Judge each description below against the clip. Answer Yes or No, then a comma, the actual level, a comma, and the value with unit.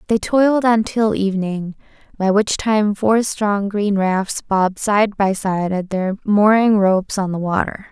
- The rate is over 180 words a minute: No, average, 175 wpm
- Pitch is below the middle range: No, high, 205 Hz